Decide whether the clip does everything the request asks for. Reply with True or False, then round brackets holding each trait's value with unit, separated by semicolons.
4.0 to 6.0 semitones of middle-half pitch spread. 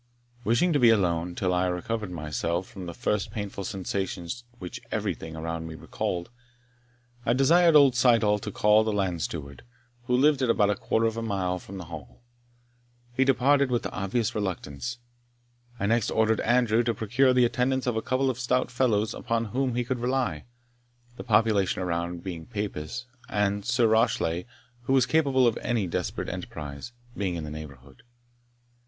True (5.6 semitones)